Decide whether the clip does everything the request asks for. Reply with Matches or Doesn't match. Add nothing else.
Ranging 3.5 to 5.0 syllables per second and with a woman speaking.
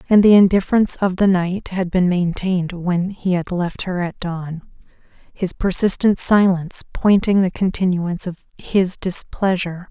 Matches